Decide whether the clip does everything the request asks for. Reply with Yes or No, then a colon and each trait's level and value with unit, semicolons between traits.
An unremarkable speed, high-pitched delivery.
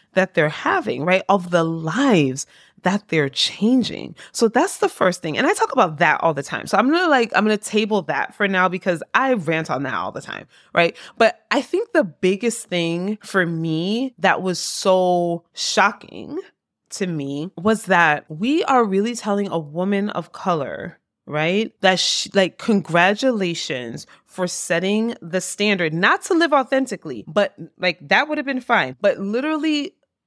Yes: average, 180 wpm; high, 195 Hz